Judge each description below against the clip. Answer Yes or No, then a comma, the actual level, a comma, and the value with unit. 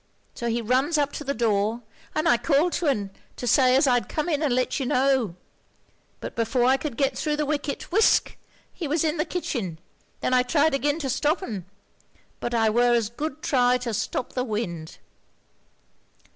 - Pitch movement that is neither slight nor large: Yes, average, 4.0 semitones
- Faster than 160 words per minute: Yes, average, 195 wpm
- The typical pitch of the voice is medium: No, very high, 255 Hz